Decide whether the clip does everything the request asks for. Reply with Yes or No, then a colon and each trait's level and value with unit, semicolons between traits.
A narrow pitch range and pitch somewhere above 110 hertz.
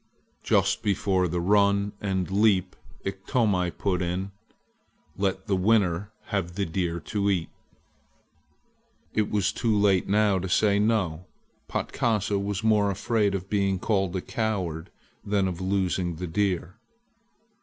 No: narrow, 2.1 semitones; low, 100 Hz